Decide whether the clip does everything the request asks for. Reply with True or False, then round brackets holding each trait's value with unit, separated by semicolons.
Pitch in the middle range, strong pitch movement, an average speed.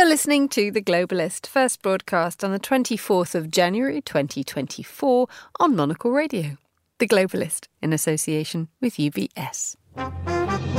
False (180 Hz; 8.0 semitones; 120 wpm)